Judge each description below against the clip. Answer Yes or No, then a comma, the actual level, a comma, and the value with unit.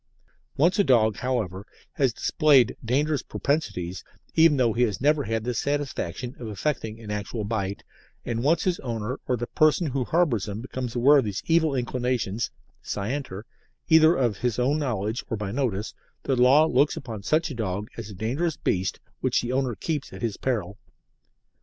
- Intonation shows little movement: No, average, 4.8 semitones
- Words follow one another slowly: No, average, 175 wpm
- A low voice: Yes, low, 125 Hz